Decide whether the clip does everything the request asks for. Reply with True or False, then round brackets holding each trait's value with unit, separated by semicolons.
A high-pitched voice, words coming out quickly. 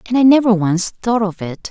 True (210 Hz; 245 wpm)